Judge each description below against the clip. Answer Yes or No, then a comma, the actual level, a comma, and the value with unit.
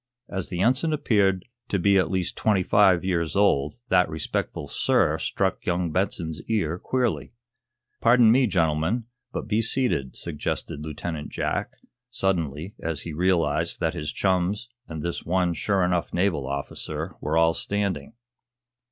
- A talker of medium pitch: No, very low, 90 Hz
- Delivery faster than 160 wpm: No, average, 145 wpm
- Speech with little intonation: No, average, 3.8 semitones